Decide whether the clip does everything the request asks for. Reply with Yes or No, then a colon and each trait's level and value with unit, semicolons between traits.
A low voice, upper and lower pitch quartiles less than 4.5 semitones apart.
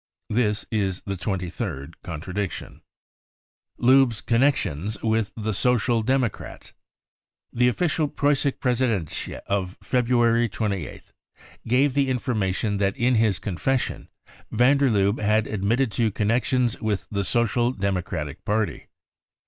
Yes: low, 110 Hz; average, 3.9 semitones